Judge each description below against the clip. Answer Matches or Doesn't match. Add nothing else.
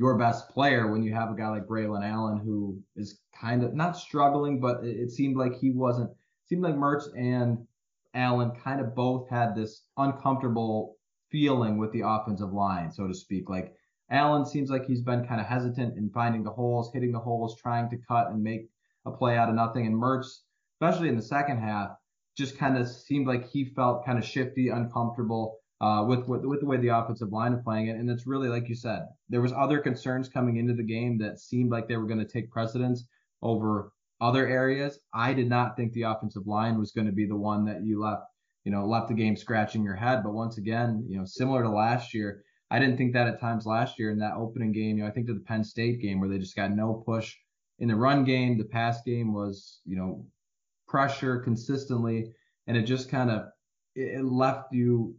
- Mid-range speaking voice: Doesn't match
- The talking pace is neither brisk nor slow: Doesn't match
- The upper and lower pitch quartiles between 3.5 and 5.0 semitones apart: Doesn't match